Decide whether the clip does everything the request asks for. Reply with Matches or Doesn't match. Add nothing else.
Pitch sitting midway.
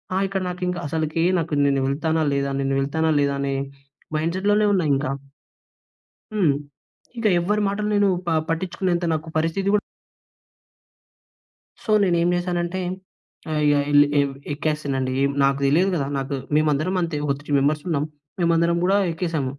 Matches